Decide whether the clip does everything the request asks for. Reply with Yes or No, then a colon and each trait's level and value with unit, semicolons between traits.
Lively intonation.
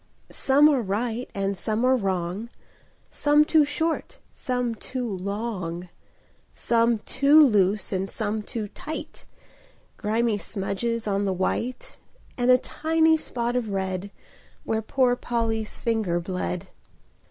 No: average, 4.2 semitones